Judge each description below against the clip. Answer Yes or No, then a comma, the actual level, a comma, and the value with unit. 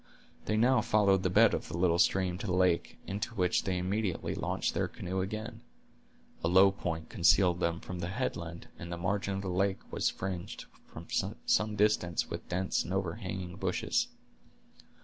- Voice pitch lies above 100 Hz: No, very low, 95 Hz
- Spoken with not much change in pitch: Yes, narrow, 2.2 semitones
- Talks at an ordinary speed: Yes, average, 175 wpm